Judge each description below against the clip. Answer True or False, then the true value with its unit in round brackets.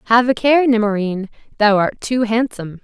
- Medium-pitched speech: False (225 Hz)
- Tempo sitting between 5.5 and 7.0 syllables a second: False (5.2 syllables/s)